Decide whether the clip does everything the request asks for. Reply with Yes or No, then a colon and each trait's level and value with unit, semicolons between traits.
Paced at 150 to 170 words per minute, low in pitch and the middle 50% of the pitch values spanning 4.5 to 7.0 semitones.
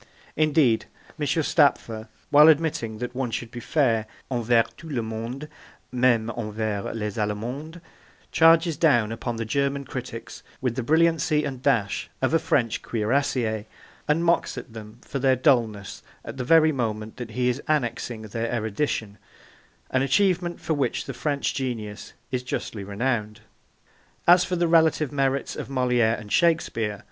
Yes: average, 155 wpm; low, 125 Hz; average, 4.8 semitones